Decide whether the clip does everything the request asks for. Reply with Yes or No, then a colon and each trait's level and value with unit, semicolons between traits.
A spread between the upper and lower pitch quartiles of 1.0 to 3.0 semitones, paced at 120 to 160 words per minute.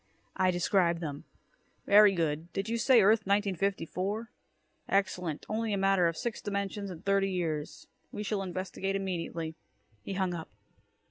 Yes: average, 2.7 semitones; average, 145 wpm